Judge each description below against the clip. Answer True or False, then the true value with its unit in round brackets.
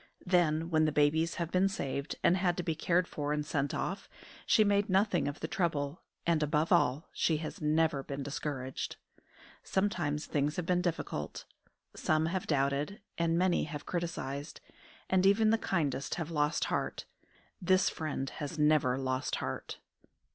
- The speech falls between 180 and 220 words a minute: False (160 wpm)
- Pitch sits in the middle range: True (160 Hz)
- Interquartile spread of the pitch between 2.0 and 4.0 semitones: True (3.5 semitones)